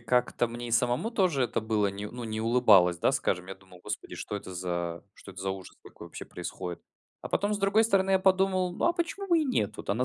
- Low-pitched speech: Yes, low, 120 Hz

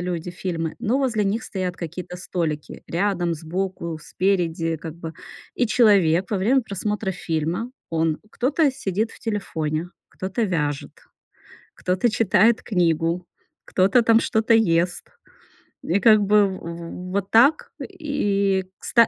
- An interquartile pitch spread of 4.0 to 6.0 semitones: Yes, average, 4.4 semitones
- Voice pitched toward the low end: No, medium, 185 Hz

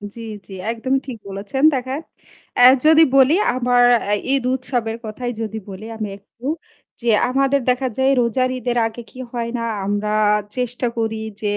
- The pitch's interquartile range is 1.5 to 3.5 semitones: Yes, average, 2.7 semitones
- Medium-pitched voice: No, high, 245 Hz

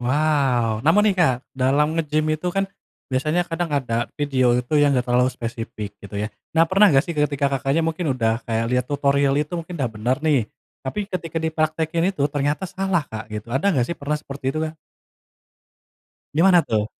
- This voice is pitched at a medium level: Yes, medium, 145 Hz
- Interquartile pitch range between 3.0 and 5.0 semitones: Yes, average, 4.6 semitones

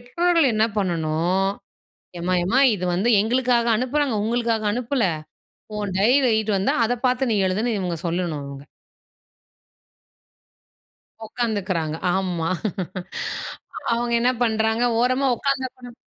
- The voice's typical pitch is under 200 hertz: No, high, 220 Hz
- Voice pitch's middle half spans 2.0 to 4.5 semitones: No, average, 5.0 semitones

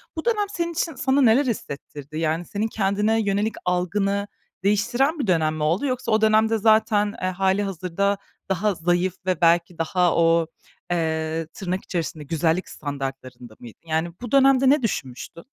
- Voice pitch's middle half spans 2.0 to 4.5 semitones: No, average, 5.1 semitones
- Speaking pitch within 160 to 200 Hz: Yes, high, 190 Hz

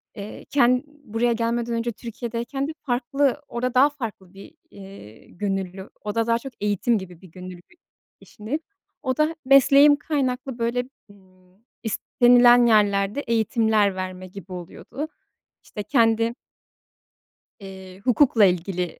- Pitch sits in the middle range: No, high, 230 Hz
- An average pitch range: Yes, average, 4.4 semitones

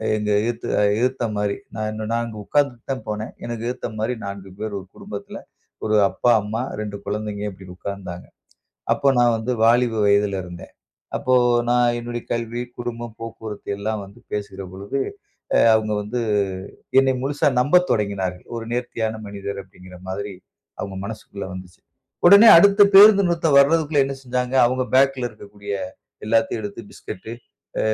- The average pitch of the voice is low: Yes, low, 110 Hz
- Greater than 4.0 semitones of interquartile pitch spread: No, average, 3.5 semitones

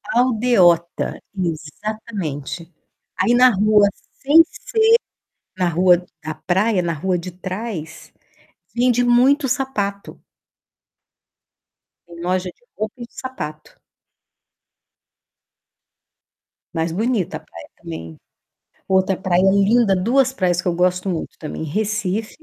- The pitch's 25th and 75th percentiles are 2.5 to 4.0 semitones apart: No, average, 5.3 semitones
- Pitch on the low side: No, high, 190 Hz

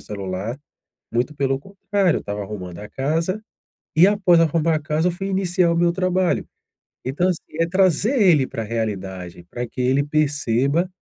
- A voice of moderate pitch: Yes, medium, 155 Hz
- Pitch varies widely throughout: Yes, wide, 7.5 semitones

